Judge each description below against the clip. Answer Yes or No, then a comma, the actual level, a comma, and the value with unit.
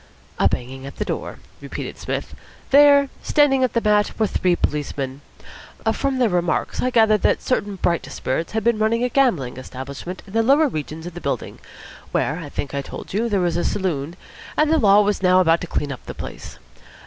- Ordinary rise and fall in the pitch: No, wide, 7.2 semitones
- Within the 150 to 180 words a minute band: No, fast, 205 wpm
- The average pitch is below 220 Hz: Yes, high, 190 Hz